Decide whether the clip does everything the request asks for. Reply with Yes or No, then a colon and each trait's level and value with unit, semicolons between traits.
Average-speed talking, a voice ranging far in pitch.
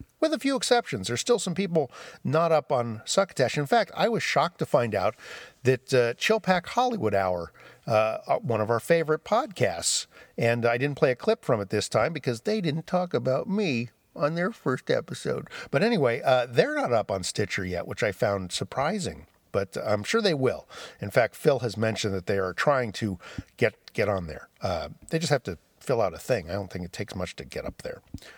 No: fast, 220 wpm; wide, 7.8 semitones